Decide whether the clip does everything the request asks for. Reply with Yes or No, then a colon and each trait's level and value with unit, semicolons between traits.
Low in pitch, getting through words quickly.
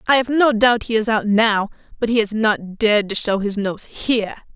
No: high, 220 Hz; fast, 235 wpm